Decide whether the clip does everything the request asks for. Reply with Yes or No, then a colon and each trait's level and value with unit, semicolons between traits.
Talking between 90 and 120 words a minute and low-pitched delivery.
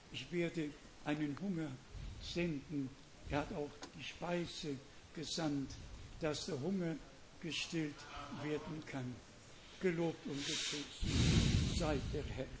No: average, 110 wpm; medium, 145 Hz